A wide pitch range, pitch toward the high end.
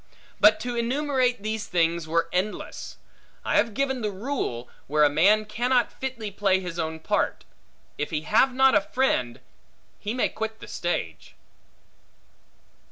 Yes: wide, 6.7 semitones; high, 210 Hz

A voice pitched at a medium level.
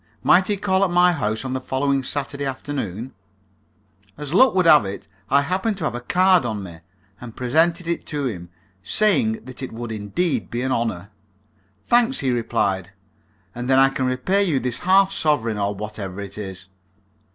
No: low, 130 Hz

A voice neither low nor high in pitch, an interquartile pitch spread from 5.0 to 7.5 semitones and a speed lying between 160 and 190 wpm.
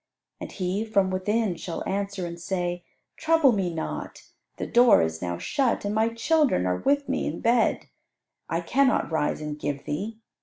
No: high, 195 Hz; wide, 5.5 semitones; average, 175 wpm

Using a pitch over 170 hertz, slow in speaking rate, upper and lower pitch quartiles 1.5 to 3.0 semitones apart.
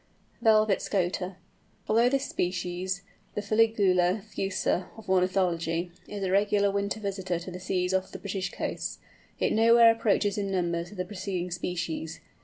No: high, 190 Hz; average, 145 wpm; narrow, 2.4 semitones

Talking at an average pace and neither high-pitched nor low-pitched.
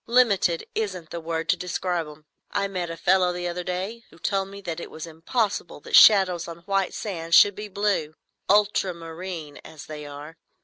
Yes: average, 175 wpm; medium, 180 Hz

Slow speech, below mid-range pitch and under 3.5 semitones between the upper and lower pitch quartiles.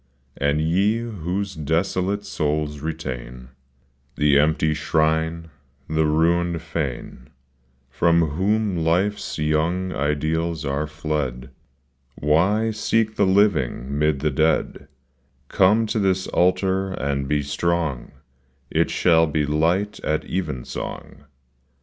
No: slow, 110 wpm; very low, 80 Hz; average, 3.8 semitones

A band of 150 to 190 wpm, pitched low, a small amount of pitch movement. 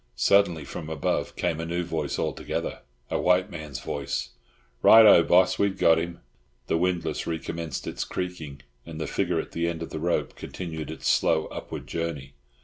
Yes: average, 175 wpm; very low, 85 Hz; narrow, 2.1 semitones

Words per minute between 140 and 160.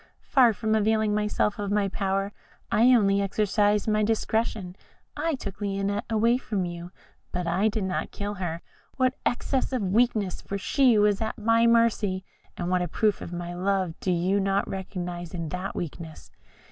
No: average, 170 wpm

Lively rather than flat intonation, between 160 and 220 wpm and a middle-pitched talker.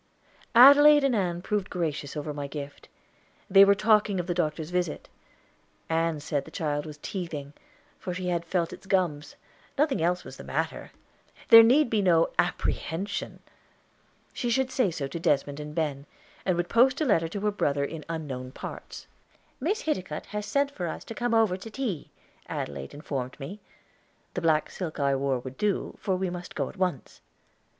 Yes: wide, 5.8 semitones; average, 180 wpm; medium, 175 Hz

